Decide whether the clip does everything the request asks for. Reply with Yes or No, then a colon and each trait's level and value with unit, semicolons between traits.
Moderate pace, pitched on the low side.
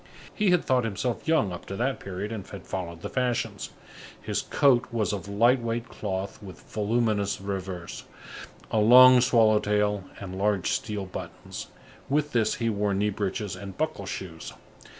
Yes: average, 165 wpm; low, 105 Hz